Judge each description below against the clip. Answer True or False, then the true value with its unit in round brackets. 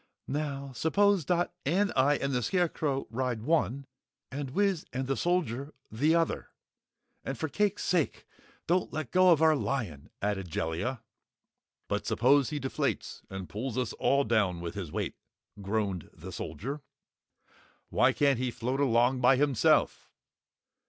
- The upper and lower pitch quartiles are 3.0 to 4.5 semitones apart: False (5.2 semitones)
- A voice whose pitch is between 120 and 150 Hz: True (135 Hz)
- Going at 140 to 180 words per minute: True (145 wpm)